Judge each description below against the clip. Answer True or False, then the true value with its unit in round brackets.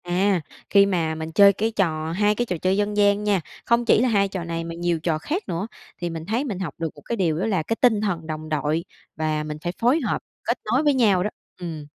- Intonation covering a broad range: False (4.4 semitones)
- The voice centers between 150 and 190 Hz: True (185 Hz)